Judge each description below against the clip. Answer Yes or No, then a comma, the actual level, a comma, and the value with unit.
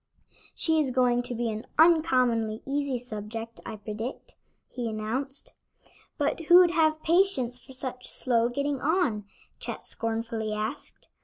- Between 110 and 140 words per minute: Yes, slow, 135 wpm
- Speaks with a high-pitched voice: Yes, very high, 250 Hz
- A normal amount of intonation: Yes, average, 4.3 semitones